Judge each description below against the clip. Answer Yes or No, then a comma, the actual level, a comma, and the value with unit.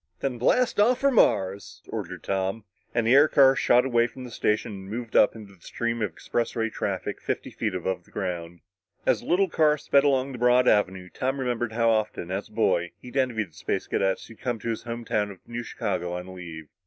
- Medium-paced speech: No, fast, 220 wpm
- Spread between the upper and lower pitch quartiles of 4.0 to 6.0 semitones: Yes, average, 4.7 semitones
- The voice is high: No, low, 115 Hz